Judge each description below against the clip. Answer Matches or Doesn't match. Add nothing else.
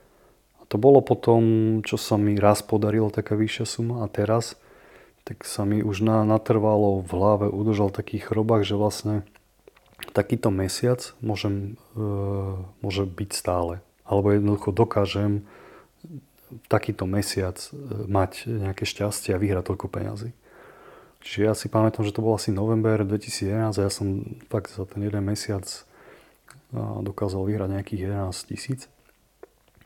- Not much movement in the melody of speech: Matches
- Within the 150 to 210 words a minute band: Doesn't match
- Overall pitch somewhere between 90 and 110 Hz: Matches